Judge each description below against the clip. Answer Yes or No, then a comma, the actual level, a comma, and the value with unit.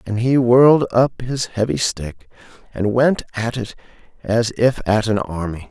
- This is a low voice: Yes, low, 115 Hz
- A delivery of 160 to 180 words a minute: Yes, average, 170 wpm